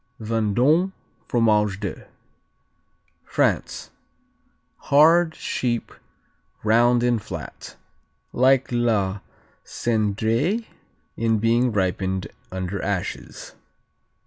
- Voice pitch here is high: No, low, 115 Hz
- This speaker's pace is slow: Yes, slow, 70 wpm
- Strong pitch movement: No, average, 3.2 semitones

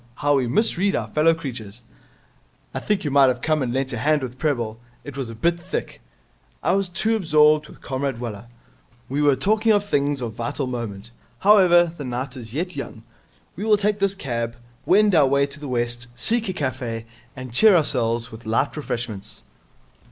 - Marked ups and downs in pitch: Yes, wide, 6.2 semitones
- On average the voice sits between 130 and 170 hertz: Yes, medium, 140 Hz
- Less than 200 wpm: Yes, average, 190 wpm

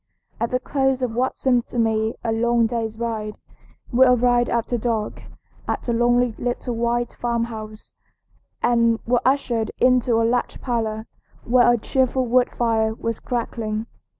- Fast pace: No, average, 150 wpm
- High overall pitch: Yes, high, 235 Hz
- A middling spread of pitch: No, narrow, 1.5 semitones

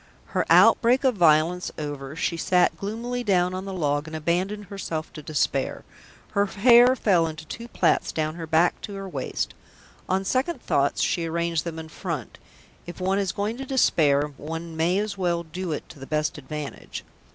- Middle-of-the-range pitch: Yes, medium, 175 Hz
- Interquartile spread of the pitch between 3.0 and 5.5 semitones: Yes, average, 4.1 semitones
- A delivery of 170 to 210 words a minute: Yes, average, 185 wpm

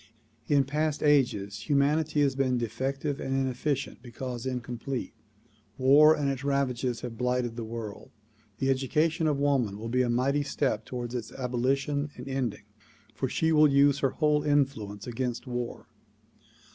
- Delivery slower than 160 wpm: Yes, average, 150 wpm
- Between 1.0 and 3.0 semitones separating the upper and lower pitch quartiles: Yes, average, 2.7 semitones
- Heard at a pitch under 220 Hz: Yes, low, 135 Hz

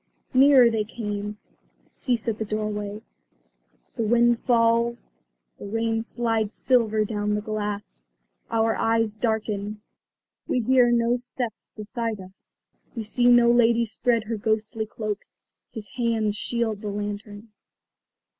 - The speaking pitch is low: No, high, 225 Hz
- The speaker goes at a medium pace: No, slow, 125 wpm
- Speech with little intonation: Yes, narrow, 2.0 semitones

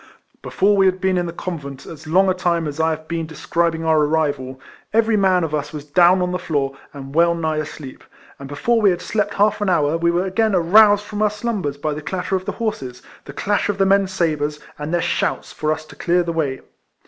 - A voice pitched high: No, medium, 170 Hz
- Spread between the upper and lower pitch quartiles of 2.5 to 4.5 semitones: Yes, average, 3.9 semitones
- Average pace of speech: No, fast, 235 wpm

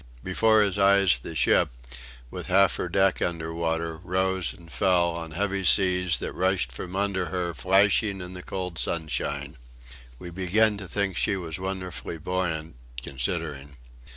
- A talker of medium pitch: No, very low, 90 Hz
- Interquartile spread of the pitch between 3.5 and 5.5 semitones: No, average, 2.8 semitones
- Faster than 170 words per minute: No, average, 155 wpm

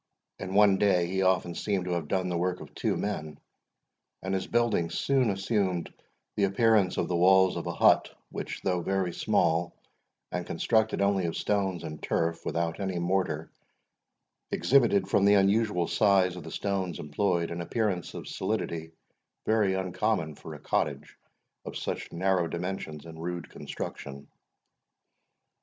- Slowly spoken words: No, average, 155 wpm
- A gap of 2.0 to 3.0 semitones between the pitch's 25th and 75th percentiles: Yes, average, 2.7 semitones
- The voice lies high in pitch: No, very low, 95 Hz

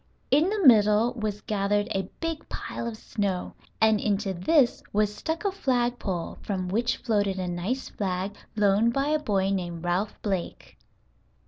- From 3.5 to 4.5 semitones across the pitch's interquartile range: Yes, average, 4.0 semitones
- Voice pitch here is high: Yes, high, 210 Hz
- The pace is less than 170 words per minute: Yes, average, 160 wpm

